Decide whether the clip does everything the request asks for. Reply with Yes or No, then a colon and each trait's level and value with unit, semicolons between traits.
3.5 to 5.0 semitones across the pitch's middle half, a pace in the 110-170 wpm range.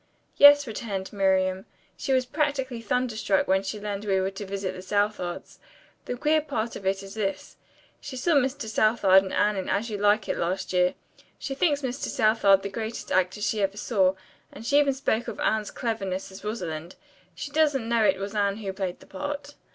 No: average, 4.5 semitones; average, 200 wpm